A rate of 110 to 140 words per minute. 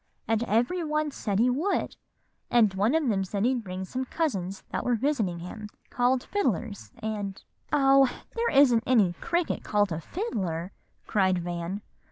No: average, 160 wpm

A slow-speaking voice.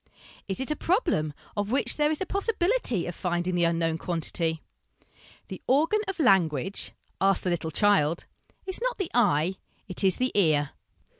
No: average, 165 wpm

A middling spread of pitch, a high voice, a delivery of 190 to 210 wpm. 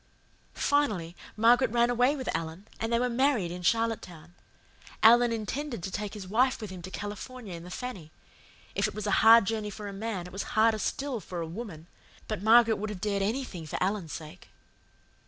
Yes: average, 4.4 semitones; high, 215 Hz; average, 195 wpm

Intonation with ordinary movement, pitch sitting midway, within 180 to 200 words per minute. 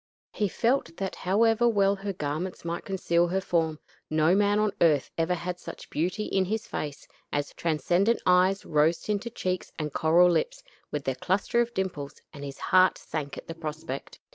Yes: average, 4.0 semitones; medium, 180 Hz; average, 185 wpm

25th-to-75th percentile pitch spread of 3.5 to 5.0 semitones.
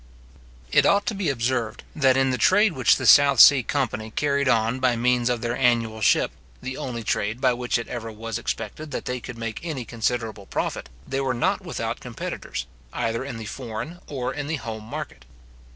No: average, 3.0 semitones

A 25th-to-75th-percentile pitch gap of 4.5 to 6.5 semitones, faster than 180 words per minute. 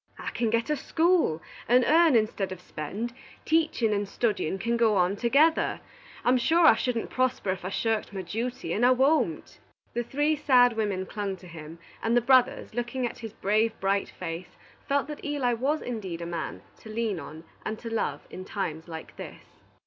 Yes: average, 5.0 semitones; average, 190 wpm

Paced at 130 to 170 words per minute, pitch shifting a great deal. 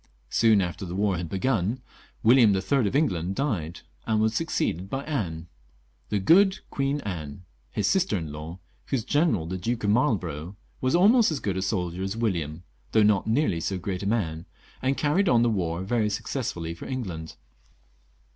No: average, 180 wpm; wide, 6.8 semitones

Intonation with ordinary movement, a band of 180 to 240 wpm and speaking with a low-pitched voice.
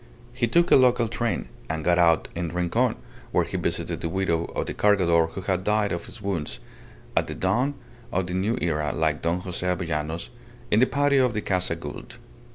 Yes: average, 4.2 semitones; average, 200 wpm; very low, 90 Hz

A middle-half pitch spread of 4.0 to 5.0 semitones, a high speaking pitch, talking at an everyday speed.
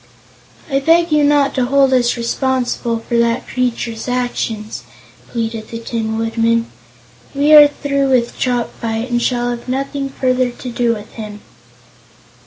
No: average, 2.8 semitones; high, 245 Hz; average, 145 wpm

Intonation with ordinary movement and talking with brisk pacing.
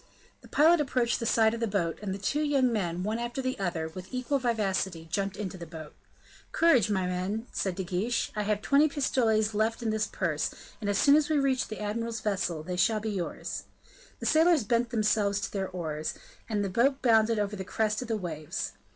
Yes: average, 4.0 semitones; fast, 215 wpm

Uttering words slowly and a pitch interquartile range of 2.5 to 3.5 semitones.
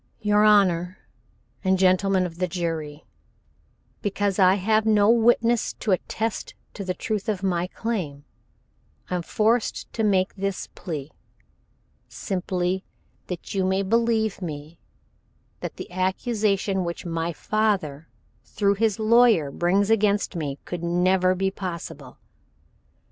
Yes: slow, 125 wpm; average, 3.1 semitones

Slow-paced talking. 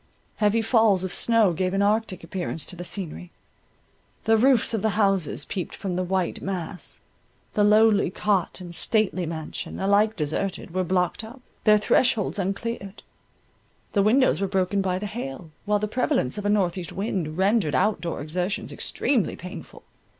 No: average, 165 wpm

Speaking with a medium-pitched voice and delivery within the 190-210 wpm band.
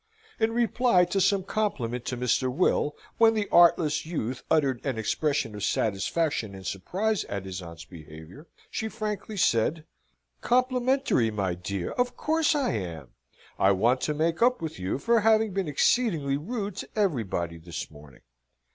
No: medium, 150 Hz; average, 155 wpm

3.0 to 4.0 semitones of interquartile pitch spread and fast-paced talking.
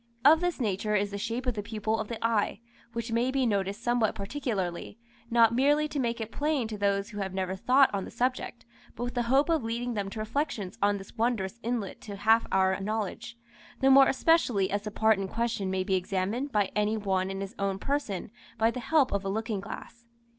Yes: average, 3.5 semitones; fast, 220 wpm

